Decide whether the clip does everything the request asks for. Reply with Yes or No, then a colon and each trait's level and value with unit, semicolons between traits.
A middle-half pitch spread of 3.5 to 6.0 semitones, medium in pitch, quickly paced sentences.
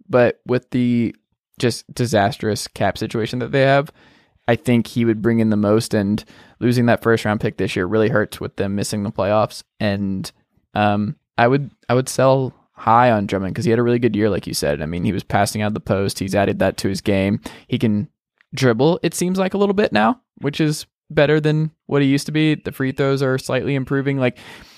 No: average, 4.7 semitones; low, 120 Hz; fast, 225 wpm